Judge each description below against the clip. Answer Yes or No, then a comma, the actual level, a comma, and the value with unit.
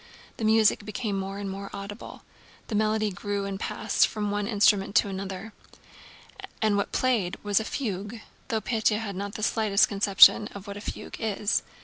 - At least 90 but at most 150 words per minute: No, average, 175 wpm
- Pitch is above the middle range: Yes, high, 205 Hz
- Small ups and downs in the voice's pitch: Yes, narrow, 1.6 semitones